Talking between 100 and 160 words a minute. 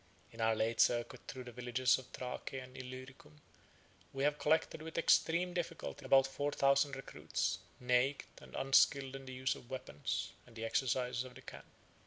No: average, 175 wpm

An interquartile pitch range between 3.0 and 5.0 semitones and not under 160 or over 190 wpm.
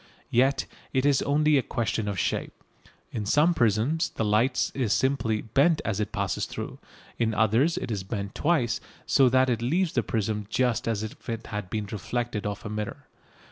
Yes: average, 4.0 semitones; average, 185 wpm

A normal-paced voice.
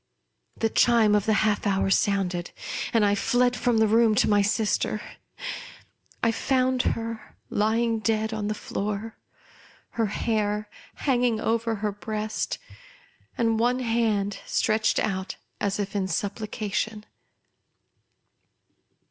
No: slow, 120 wpm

